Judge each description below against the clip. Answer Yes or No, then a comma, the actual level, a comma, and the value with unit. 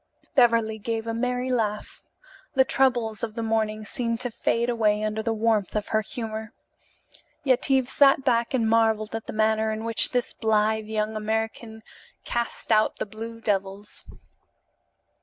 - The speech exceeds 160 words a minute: No, average, 155 wpm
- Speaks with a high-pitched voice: Yes, high, 225 Hz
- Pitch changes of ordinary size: No, narrow, 1.5 semitones